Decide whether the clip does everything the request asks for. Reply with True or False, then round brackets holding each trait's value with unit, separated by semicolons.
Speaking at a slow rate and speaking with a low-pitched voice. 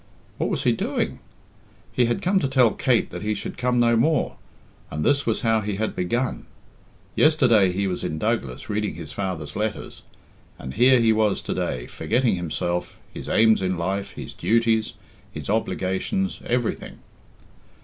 False (165 wpm; 110 Hz)